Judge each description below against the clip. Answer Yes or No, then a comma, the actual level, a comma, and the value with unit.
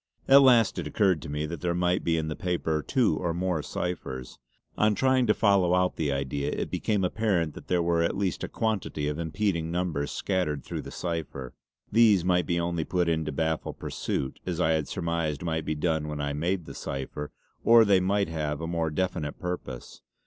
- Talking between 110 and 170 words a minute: No, fast, 205 wpm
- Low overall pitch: Yes, very low, 85 Hz